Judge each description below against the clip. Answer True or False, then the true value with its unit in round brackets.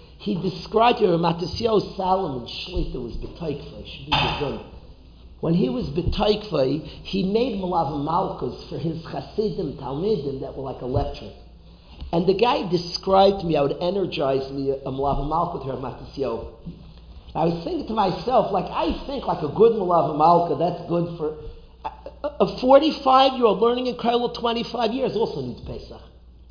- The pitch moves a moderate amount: False (7.9 semitones)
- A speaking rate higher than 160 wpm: False (145 wpm)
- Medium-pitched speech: True (175 Hz)